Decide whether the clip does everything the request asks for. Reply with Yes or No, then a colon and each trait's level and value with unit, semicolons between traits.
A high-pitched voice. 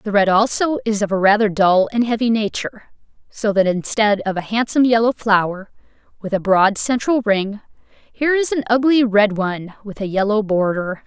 Yes: high, 215 Hz